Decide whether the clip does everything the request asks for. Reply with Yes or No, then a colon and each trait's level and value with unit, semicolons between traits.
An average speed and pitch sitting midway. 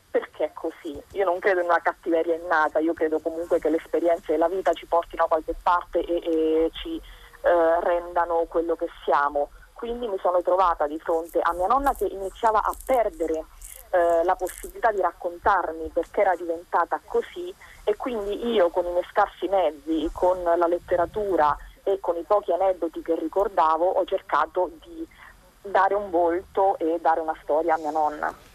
No: fast, 175 wpm; medium, 175 Hz